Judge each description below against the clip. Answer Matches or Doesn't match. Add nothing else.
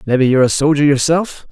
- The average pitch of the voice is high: Doesn't match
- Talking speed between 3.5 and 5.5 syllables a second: Doesn't match